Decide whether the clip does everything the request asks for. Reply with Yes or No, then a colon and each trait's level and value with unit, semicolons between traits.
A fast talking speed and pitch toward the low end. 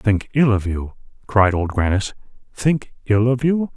No: average, 175 wpm; low, 115 Hz